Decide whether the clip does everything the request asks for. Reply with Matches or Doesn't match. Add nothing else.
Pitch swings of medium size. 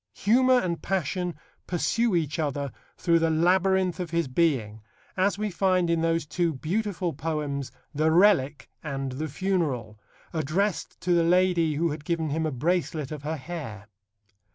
Matches